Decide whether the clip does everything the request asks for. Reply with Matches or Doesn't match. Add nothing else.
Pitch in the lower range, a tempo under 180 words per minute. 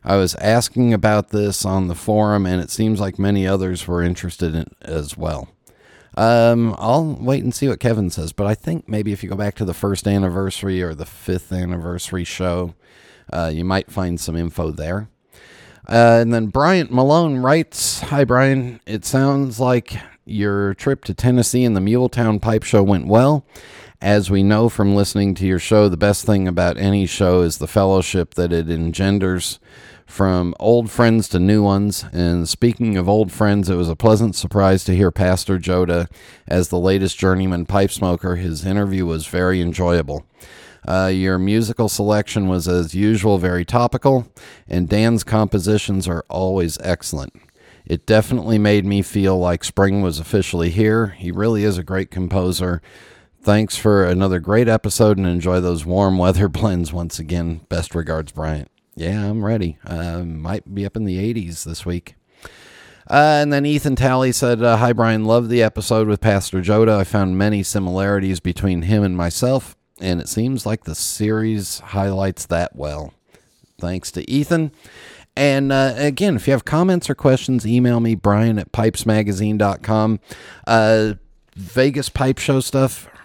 Matches